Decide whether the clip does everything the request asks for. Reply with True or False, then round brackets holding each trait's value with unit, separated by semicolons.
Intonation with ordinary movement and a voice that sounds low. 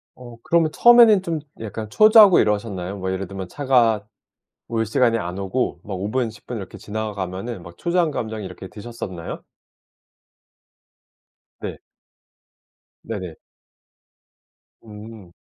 True (4.5 semitones; 110 Hz)